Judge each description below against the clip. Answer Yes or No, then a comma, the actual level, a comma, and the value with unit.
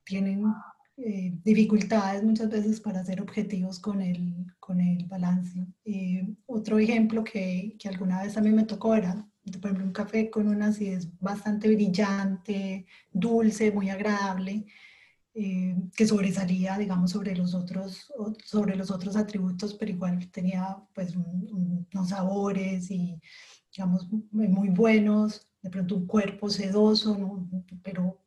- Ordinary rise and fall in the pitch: No, narrow, 2.2 semitones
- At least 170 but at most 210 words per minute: No, average, 145 wpm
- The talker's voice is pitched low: No, high, 195 Hz